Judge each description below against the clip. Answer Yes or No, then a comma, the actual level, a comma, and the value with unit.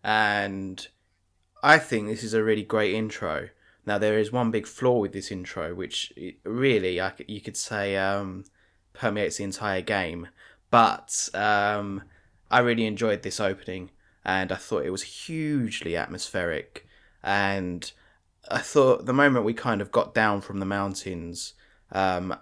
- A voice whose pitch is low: Yes, low, 100 Hz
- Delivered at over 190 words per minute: No, average, 155 wpm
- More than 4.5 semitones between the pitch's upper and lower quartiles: No, narrow, 2.6 semitones